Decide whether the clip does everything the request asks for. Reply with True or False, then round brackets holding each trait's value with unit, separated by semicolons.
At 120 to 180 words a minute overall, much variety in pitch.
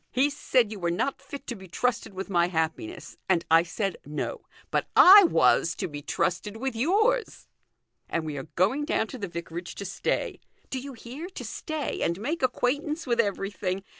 False (190 wpm; 8.1 semitones)